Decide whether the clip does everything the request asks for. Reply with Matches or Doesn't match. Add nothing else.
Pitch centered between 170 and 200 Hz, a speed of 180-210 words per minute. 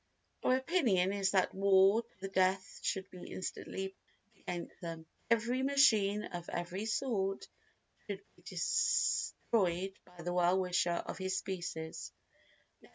Doesn't match